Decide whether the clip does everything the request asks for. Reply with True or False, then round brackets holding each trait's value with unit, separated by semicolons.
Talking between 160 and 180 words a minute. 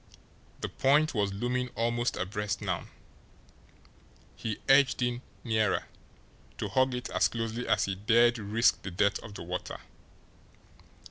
False (135 wpm)